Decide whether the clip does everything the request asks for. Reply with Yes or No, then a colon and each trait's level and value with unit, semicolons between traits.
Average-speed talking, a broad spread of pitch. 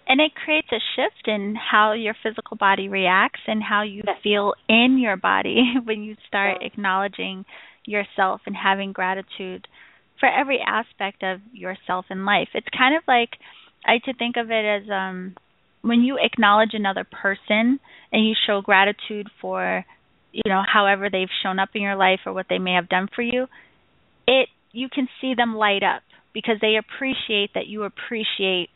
No: average, 175 wpm; average, 3.4 semitones